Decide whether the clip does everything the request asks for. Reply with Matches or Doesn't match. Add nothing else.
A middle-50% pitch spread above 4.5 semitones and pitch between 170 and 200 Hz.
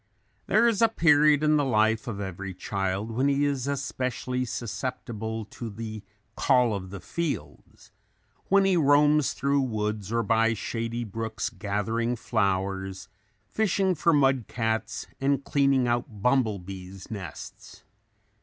Doesn't match